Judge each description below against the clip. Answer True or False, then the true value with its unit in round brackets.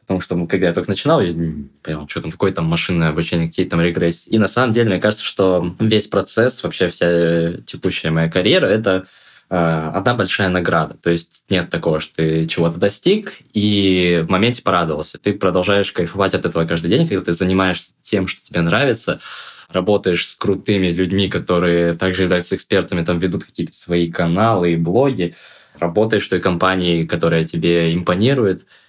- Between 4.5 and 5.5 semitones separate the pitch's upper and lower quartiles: False (2.5 semitones)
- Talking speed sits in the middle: False (175 wpm)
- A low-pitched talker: True (90 Hz)